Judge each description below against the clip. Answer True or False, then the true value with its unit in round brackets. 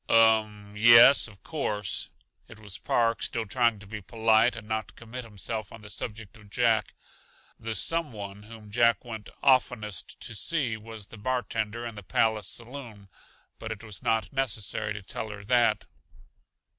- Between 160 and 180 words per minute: True (170 wpm)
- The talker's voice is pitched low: True (110 Hz)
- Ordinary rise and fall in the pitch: False (1.9 semitones)